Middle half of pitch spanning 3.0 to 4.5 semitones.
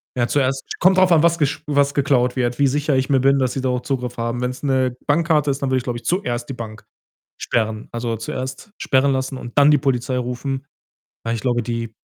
No: narrow, 2.6 semitones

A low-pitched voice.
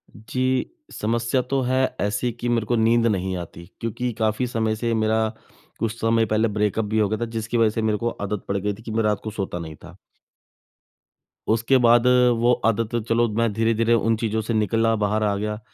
Yes: low, 110 Hz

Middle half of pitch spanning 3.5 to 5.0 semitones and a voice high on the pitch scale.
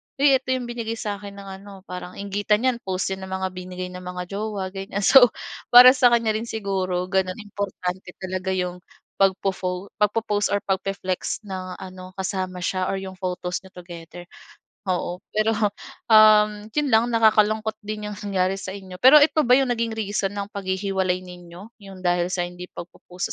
No: average, 2.7 semitones; high, 195 Hz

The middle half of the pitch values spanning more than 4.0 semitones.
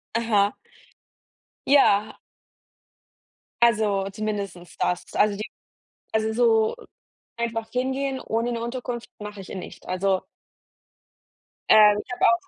No: narrow, 2.6 semitones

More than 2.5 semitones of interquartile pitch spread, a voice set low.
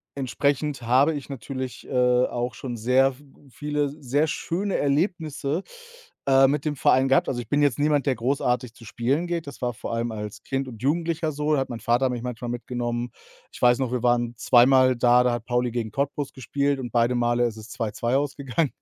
Yes: average, 2.9 semitones; low, 130 Hz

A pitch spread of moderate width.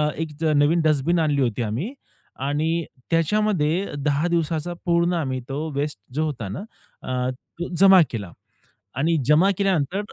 Yes: average, 3.5 semitones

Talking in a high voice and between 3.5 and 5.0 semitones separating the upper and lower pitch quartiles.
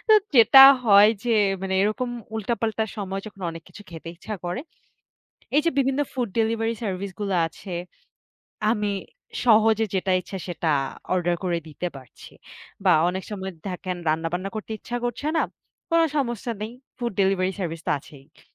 Yes: high, 200 Hz; average, 3.9 semitones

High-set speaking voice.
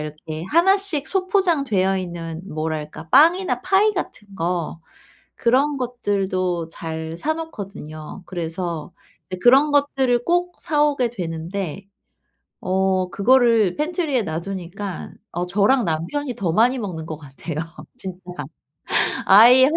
Yes: high, 195 Hz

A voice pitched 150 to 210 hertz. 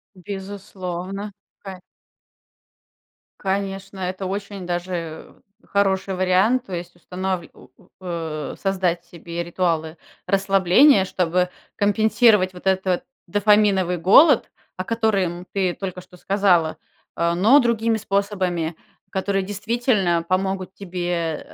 Yes: high, 190 Hz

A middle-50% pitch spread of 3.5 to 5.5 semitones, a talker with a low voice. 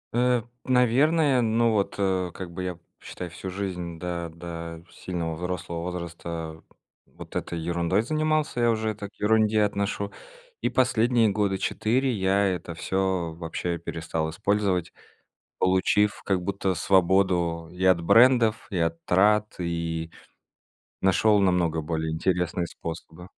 Yes: average, 3.9 semitones; very low, 95 Hz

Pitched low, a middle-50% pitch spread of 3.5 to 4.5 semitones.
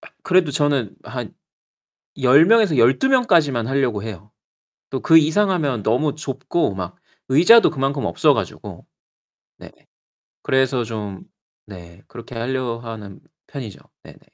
No: low, 130 Hz; average, 5.3 semitones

